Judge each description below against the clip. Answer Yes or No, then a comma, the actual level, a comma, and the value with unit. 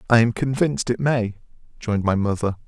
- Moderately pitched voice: No, low, 115 Hz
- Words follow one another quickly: No, average, 180 wpm